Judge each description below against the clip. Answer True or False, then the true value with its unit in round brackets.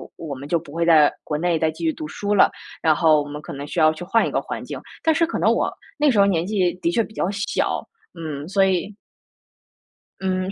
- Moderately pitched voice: True (175 Hz)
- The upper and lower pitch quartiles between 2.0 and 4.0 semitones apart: False (4.6 semitones)